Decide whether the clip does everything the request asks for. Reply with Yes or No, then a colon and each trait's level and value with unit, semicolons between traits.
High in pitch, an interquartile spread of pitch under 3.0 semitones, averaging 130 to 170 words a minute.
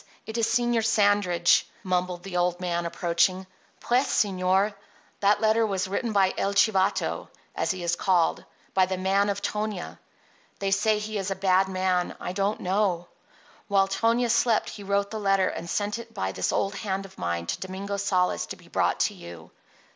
No: high, 195 Hz; narrow, 2.4 semitones; average, 185 wpm